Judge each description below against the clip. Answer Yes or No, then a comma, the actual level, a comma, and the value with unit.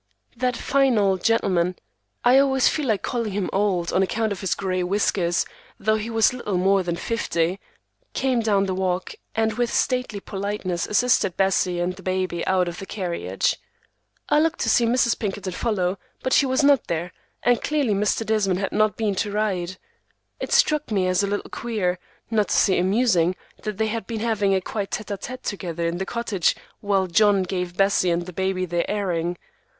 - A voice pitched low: No, high, 200 Hz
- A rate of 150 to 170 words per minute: No, average, 190 wpm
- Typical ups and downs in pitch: Yes, average, 3.6 semitones